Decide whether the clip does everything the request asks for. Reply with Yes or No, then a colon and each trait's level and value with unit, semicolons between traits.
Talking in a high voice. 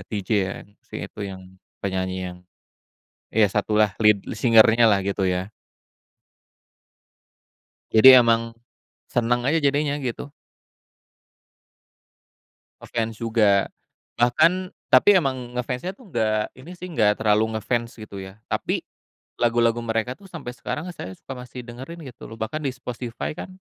No: low, 115 Hz